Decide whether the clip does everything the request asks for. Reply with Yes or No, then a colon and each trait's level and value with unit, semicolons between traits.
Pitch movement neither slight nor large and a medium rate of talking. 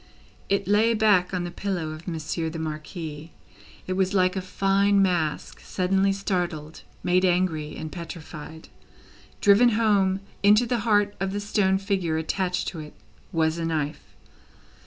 Yes: average, 3.6 semitones; average, 150 wpm